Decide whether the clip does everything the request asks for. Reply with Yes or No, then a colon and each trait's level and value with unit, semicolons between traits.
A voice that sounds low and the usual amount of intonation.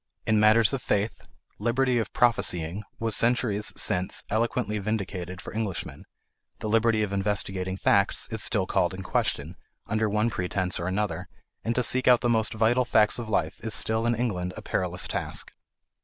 Yes: low, 110 Hz; average, 3.1 semitones